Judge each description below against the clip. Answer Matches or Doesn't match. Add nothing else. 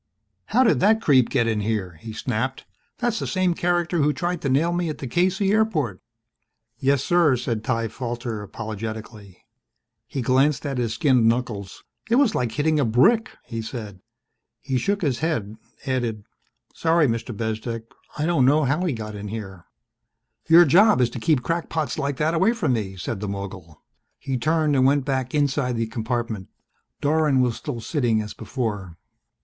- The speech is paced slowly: Doesn't match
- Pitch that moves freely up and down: Matches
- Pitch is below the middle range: Matches